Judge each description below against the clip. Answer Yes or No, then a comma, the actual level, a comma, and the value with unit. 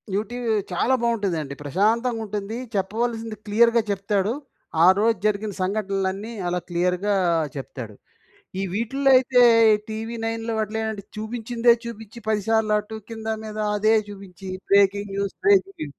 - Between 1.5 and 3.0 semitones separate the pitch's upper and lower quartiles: Yes, narrow, 2.6 semitones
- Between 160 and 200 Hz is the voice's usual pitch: No, high, 215 Hz